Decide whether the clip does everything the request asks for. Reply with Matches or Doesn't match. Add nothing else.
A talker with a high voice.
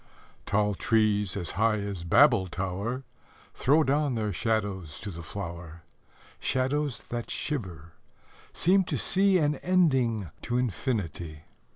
Doesn't match